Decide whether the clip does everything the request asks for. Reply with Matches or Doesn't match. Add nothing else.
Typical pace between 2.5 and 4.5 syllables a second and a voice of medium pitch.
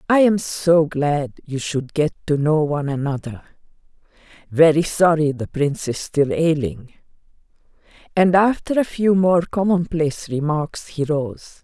Matches